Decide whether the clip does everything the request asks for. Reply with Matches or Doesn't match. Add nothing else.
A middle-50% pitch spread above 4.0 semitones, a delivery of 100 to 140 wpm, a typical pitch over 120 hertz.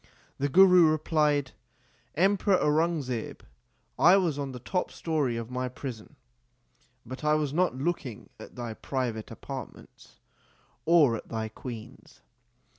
Matches